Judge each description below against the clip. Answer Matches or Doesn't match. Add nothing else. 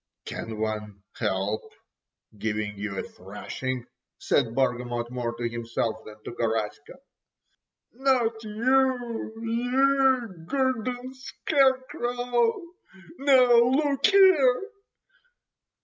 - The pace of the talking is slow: Matches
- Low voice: Doesn't match